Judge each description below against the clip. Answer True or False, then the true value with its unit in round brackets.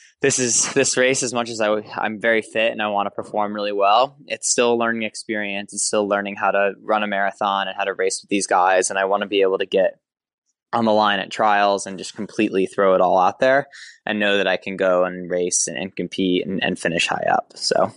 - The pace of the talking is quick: True (255 wpm)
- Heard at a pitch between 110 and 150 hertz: False (100 Hz)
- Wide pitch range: False (2.4 semitones)